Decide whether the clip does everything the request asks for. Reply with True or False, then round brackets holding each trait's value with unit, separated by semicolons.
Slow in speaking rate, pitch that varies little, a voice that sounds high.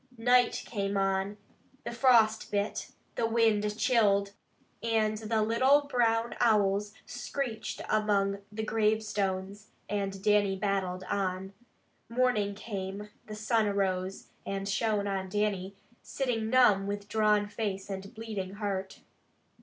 True (120 wpm; 2.1 semitones; 210 Hz)